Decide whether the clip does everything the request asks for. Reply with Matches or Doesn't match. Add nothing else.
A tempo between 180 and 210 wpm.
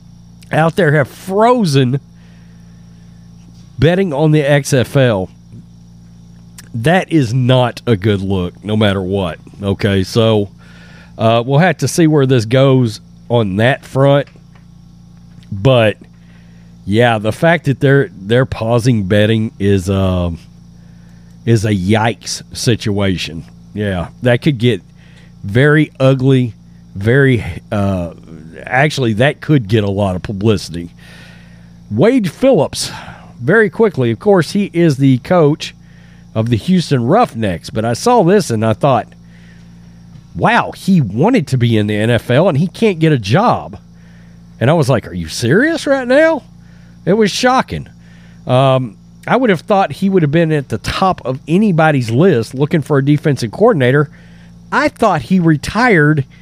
Doesn't match